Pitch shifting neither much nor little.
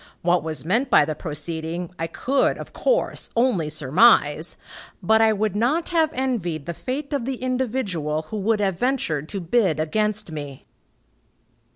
No: wide, 7.5 semitones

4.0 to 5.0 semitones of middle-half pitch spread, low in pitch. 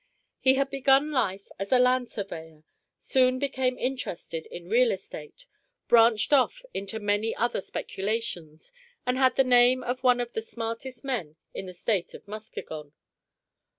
No: average, 4.3 semitones; high, 245 Hz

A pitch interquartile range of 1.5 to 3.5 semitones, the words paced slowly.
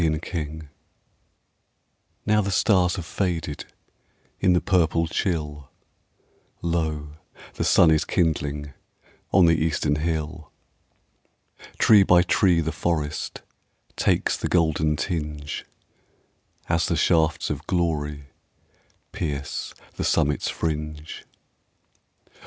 Yes: narrow, 2.5 semitones; slow, 100 wpm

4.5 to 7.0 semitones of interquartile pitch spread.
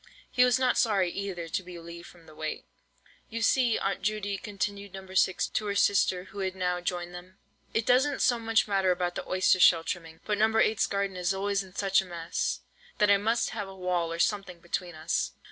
No: average, 2.8 semitones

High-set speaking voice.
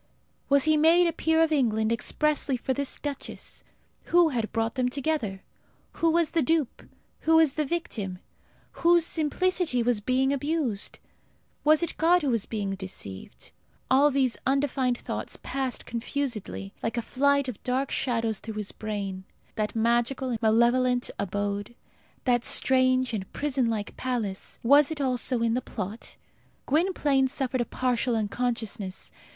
Yes: very high, 255 Hz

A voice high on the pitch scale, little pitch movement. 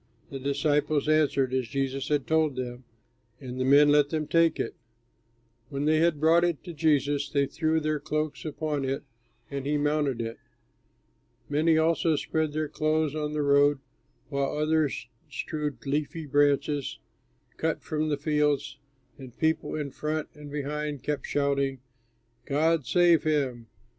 No: medium, 150 Hz; narrow, 1.9 semitones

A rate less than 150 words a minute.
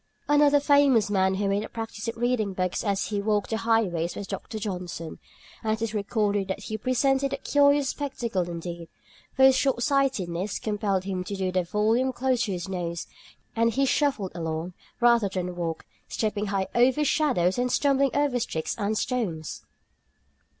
No: average, 170 wpm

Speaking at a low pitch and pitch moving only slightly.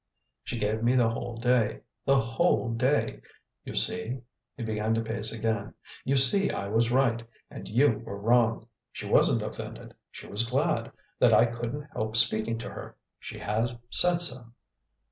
Yes: low, 115 Hz; narrow, 2.2 semitones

